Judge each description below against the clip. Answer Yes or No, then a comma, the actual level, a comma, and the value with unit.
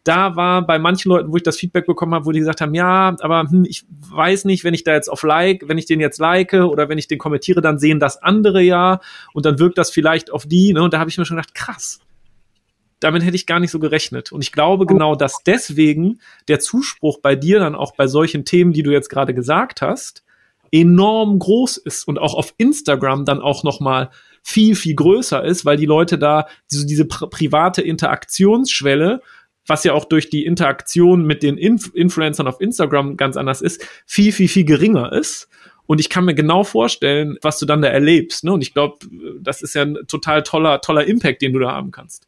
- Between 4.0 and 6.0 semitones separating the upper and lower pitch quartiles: No, average, 3.4 semitones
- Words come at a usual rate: No, fast, 225 wpm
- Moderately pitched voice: Yes, medium, 160 Hz